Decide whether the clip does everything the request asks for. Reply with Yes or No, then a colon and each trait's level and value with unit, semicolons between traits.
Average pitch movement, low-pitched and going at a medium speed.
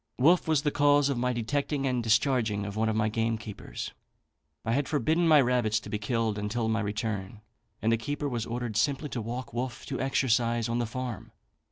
Yes: average, 3.4 semitones; low, 120 Hz; average, 195 wpm